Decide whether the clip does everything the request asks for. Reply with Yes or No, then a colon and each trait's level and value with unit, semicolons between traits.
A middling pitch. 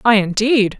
No: high, 220 Hz